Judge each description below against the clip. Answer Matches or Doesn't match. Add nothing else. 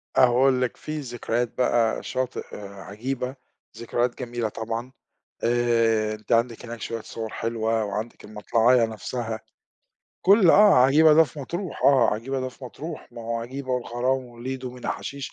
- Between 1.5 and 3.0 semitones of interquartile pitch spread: Matches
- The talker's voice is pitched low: Matches